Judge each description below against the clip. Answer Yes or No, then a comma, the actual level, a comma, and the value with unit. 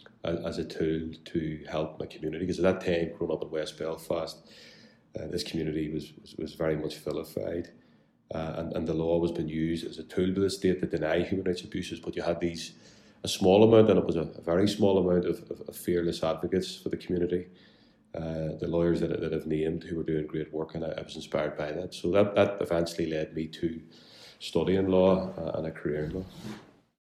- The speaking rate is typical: No, fast, 230 wpm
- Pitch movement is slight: Yes, narrow, 2.2 semitones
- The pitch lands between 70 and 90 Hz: Yes, very low, 85 Hz